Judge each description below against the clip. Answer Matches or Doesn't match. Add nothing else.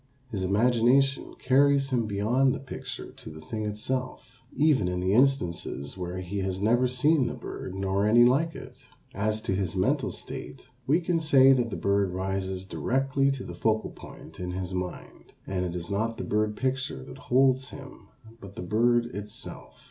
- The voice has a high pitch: Doesn't match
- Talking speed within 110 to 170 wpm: Doesn't match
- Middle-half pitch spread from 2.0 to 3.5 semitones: Doesn't match